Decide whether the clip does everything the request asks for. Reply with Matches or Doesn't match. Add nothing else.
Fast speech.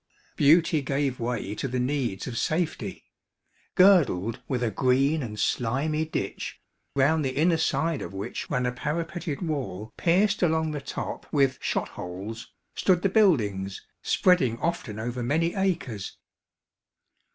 Doesn't match